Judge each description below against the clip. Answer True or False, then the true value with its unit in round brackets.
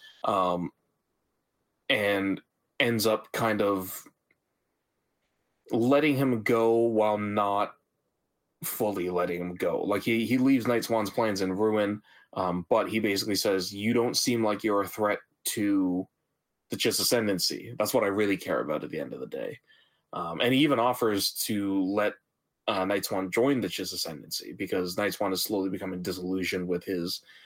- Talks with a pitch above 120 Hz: False (100 Hz)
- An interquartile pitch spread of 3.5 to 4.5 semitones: False (3.1 semitones)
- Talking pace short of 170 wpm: True (160 wpm)